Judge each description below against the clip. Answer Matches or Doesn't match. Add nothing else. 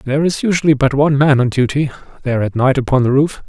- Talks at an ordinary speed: Doesn't match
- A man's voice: Matches